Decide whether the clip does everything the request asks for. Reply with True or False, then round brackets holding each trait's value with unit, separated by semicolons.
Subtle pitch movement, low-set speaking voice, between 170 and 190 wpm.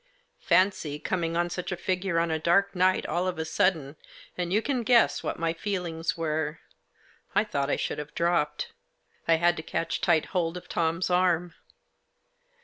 False (2.2 semitones; 170 Hz; 175 wpm)